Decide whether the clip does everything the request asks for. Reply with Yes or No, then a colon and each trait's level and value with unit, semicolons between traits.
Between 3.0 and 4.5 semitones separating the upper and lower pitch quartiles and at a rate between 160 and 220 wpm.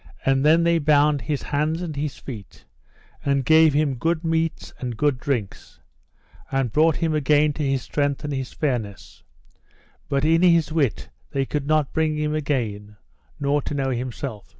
No: narrow, 2.5 semitones; average, 170 wpm